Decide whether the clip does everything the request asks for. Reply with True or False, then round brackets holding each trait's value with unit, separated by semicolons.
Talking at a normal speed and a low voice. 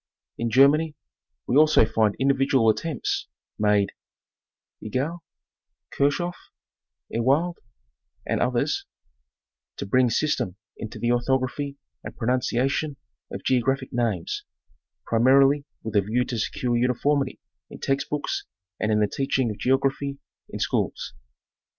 False (120 wpm; 130 Hz)